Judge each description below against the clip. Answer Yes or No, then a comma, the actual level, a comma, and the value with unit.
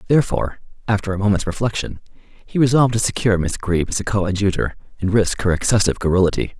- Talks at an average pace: Yes, average, 175 wpm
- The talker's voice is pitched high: No, low, 100 Hz